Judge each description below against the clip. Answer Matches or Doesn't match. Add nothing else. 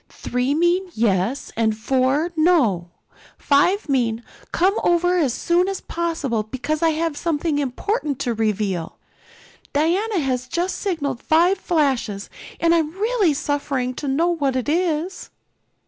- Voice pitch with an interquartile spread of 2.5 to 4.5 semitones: Doesn't match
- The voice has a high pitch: Matches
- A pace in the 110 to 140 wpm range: Matches